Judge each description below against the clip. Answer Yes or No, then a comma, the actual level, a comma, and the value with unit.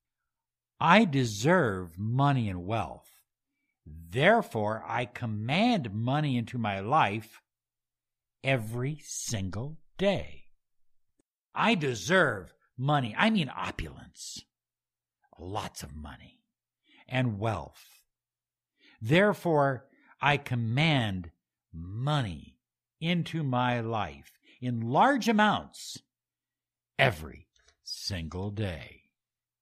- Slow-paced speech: Yes, slow, 80 wpm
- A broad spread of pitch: Yes, wide, 7.4 semitones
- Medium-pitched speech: No, low, 120 Hz